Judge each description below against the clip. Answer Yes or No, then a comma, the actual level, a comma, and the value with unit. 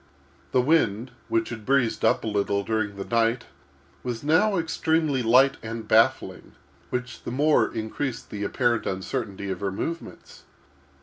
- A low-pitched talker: Yes, low, 115 Hz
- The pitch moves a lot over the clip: No, average, 4.2 semitones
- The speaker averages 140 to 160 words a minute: Yes, average, 145 wpm